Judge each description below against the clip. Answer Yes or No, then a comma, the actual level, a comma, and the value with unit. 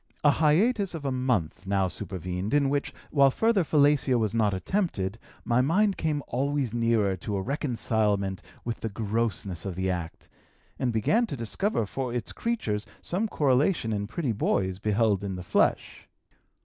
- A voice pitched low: Yes, low, 115 Hz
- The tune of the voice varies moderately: No, wide, 6.4 semitones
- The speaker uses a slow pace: No, average, 160 wpm